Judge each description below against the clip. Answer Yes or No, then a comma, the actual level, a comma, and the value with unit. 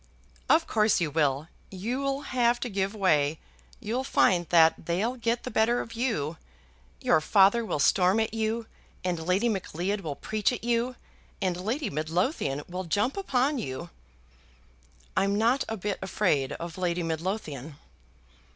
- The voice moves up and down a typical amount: No, wide, 5.7 semitones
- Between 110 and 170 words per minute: Yes, average, 150 wpm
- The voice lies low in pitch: No, high, 195 Hz